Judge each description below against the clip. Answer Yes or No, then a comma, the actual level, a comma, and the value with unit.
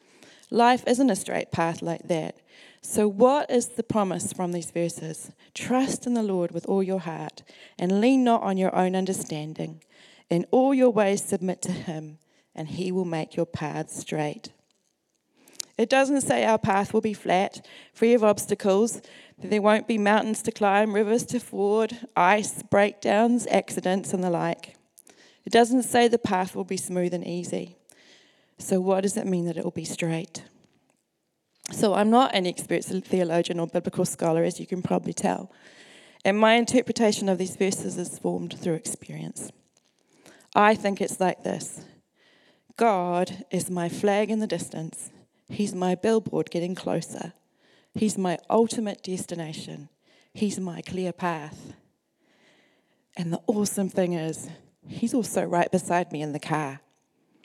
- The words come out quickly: No, average, 160 wpm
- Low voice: No, high, 190 Hz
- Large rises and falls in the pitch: No, average, 4.2 semitones